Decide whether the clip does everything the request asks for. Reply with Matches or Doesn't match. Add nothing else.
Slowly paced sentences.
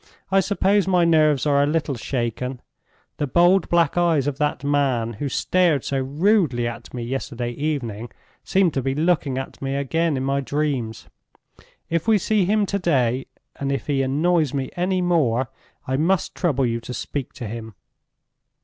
Doesn't match